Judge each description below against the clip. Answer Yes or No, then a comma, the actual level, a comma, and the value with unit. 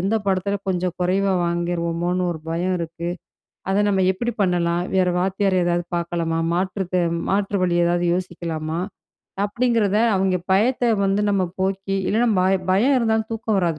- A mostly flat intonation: Yes, narrow, 2.3 semitones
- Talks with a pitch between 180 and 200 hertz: Yes, medium, 185 Hz